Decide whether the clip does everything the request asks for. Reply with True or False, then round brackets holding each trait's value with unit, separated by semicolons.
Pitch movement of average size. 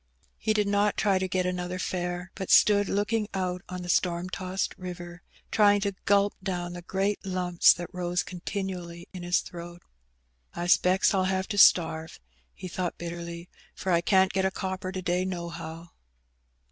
False (1.6 semitones)